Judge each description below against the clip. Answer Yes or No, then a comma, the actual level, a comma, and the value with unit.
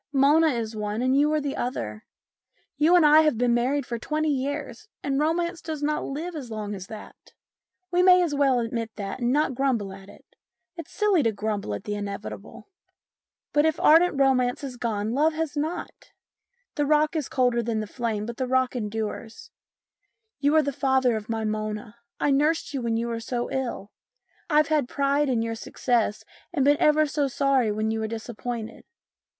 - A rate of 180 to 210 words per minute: Yes, average, 190 wpm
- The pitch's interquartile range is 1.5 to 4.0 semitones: No, average, 4.9 semitones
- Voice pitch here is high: Yes, very high, 260 Hz